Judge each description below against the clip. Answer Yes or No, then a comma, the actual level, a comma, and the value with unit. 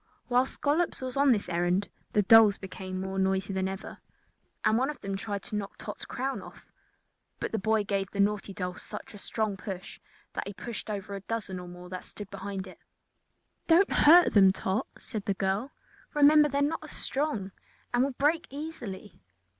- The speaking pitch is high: Yes, high, 205 Hz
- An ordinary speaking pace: Yes, average, 190 wpm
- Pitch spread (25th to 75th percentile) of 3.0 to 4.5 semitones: No, wide, 5.4 semitones